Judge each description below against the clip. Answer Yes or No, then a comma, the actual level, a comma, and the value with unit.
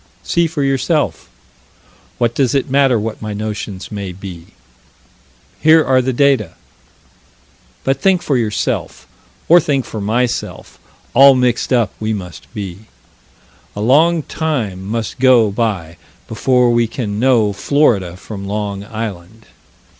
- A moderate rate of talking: No, slow, 130 wpm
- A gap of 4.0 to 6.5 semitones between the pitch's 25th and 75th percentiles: Yes, average, 4.6 semitones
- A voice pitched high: No, low, 115 Hz